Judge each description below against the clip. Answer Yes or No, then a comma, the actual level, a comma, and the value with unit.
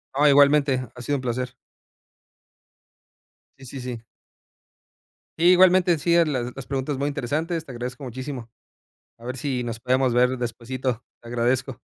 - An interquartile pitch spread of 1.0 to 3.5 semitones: Yes, average, 2.7 semitones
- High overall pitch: No, low, 130 Hz